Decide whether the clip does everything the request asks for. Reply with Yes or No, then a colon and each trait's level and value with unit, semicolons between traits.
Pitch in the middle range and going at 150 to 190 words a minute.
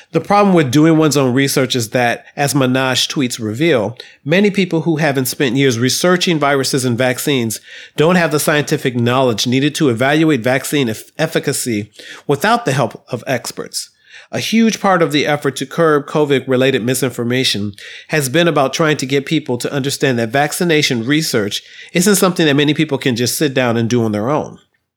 Yes: medium, 145 Hz; average, 180 wpm